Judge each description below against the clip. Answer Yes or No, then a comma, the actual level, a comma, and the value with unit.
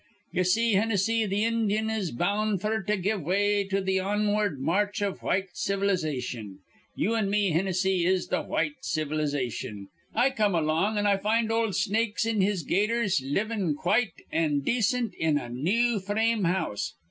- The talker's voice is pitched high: Yes, high, 200 Hz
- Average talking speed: Yes, average, 160 wpm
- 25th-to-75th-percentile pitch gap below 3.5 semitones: No, average, 4.1 semitones